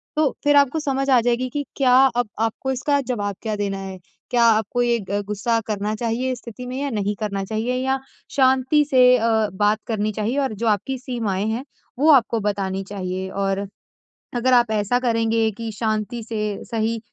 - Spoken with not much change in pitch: No, average, 3.4 semitones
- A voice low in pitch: No, high, 230 Hz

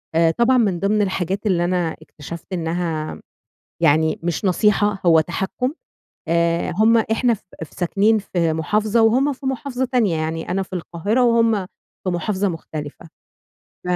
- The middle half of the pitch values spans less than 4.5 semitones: No, average, 4.9 semitones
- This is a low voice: No, high, 190 Hz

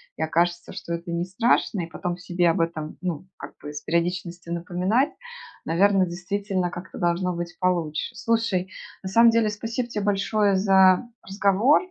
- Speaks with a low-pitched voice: No, medium, 185 Hz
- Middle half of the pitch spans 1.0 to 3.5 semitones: Yes, average, 3.0 semitones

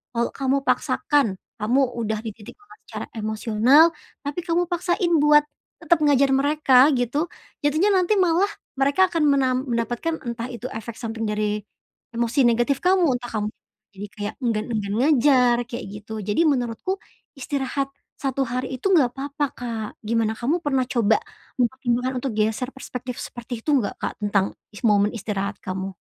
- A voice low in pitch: No, very high, 250 Hz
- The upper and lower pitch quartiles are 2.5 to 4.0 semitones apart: No, average, 4.5 semitones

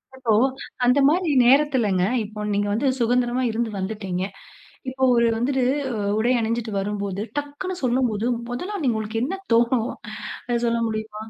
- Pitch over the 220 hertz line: Yes, high, 235 Hz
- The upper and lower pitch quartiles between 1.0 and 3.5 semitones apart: Yes, average, 3.2 semitones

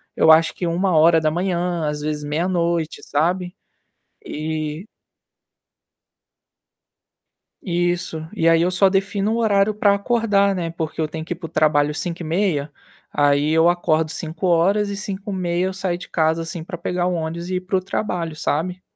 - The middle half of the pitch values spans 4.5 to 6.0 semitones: No, average, 2.8 semitones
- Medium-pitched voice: Yes, medium, 170 Hz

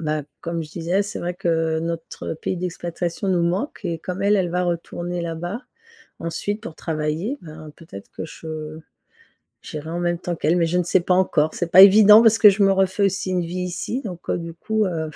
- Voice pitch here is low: No, medium, 175 Hz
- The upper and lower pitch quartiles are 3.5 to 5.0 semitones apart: No, narrow, 2.6 semitones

